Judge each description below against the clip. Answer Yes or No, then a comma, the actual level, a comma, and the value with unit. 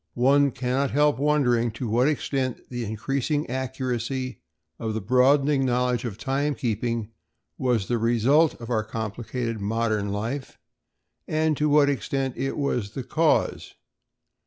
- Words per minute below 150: Yes, slow, 135 wpm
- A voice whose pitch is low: Yes, low, 125 Hz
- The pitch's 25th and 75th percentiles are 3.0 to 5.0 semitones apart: Yes, average, 3.3 semitones